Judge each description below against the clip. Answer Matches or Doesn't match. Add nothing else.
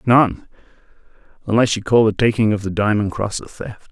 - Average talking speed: Matches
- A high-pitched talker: Doesn't match